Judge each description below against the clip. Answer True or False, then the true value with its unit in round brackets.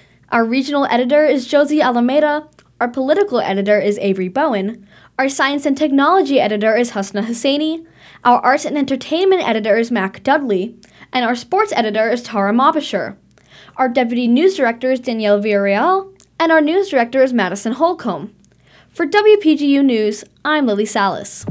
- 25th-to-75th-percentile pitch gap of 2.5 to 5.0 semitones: False (5.6 semitones)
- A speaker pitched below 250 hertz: False (255 Hz)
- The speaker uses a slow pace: False (155 wpm)